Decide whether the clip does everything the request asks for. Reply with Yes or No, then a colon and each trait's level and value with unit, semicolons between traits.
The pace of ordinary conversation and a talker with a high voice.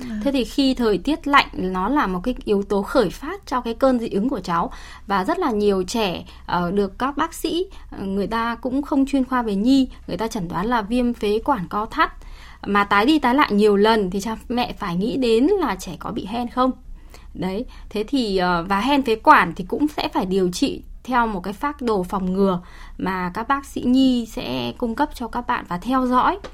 Yes: average, 230 wpm; high, 230 Hz